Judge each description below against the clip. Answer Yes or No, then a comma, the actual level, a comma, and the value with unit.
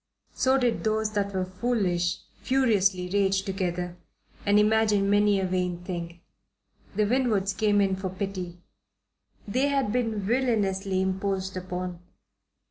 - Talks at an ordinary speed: No, slow, 125 wpm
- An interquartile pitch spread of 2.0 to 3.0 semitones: Yes, average, 2.7 semitones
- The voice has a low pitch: No, high, 195 Hz